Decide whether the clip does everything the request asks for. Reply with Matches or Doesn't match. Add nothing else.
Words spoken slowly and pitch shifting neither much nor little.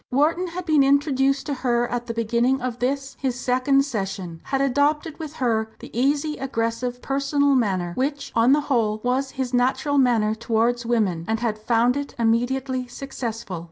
Doesn't match